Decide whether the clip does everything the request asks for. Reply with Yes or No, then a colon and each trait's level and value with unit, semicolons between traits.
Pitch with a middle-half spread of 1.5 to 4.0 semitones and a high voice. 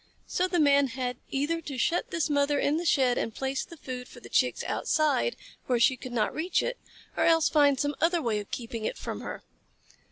No: average, 4.6 semitones; very high, 285 Hz